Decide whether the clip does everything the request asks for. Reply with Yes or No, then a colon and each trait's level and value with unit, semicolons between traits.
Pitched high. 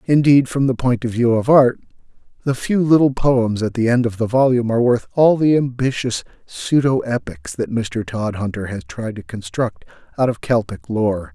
No: low, 115 Hz